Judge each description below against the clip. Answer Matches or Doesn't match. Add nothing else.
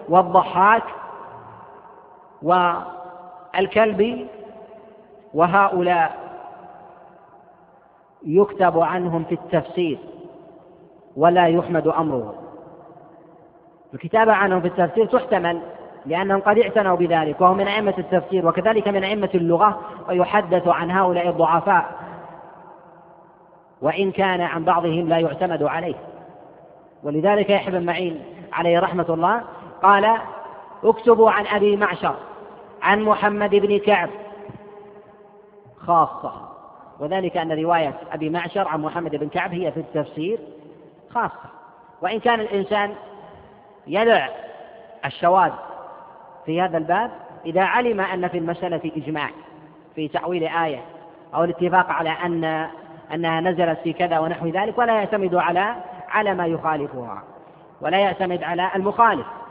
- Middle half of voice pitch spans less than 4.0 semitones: Matches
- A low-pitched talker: Doesn't match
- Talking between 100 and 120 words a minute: Matches